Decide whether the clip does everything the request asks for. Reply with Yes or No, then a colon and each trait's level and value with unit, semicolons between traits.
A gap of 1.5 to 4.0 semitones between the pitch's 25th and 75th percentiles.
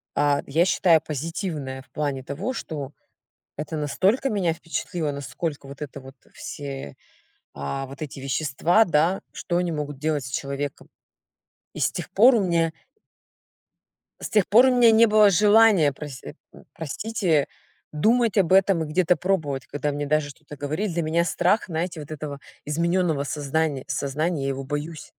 No: average, 4.4 semitones